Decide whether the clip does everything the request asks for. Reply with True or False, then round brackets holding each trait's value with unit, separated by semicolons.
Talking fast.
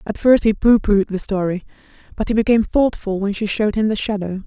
True (230 wpm)